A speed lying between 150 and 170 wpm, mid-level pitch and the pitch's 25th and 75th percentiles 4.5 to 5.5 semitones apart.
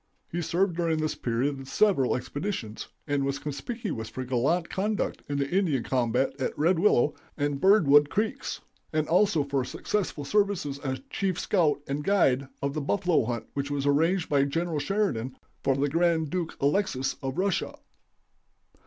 Yes: average, 160 wpm; medium, 145 Hz; average, 4.8 semitones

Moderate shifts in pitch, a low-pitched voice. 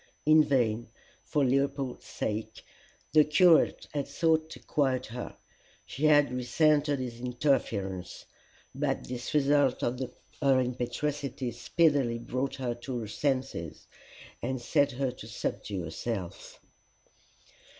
Yes: average, 3.3 semitones; low, 130 Hz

